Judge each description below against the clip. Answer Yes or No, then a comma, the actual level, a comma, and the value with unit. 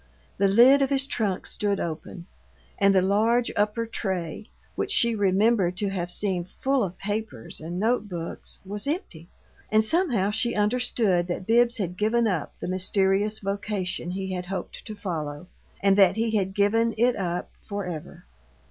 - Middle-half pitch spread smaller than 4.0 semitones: Yes, average, 3.6 semitones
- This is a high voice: Yes, high, 200 Hz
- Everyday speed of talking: Yes, average, 165 wpm